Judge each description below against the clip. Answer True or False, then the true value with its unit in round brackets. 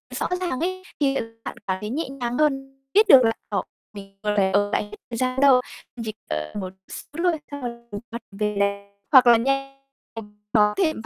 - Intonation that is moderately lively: True (4.8 semitones)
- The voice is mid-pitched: False (245 Hz)